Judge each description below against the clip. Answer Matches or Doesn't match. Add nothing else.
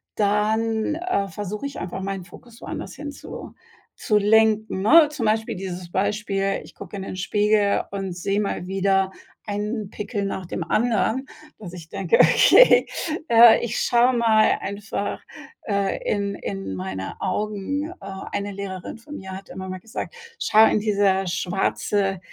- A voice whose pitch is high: Matches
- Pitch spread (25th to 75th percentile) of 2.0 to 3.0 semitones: Matches